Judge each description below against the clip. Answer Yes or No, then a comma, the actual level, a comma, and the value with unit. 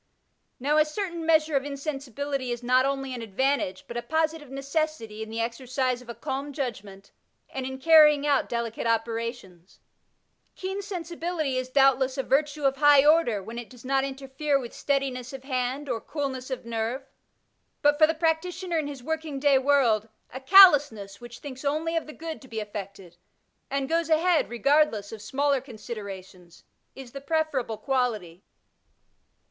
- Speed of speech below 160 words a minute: No, average, 165 wpm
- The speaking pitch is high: Yes, very high, 270 Hz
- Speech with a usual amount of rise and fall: Yes, average, 4.1 semitones